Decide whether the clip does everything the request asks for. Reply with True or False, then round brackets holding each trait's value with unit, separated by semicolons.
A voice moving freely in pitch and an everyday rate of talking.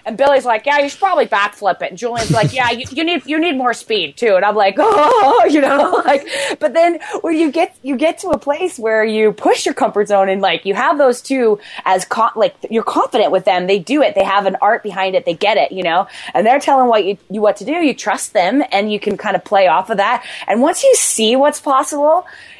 False (6.5 semitones; 260 wpm)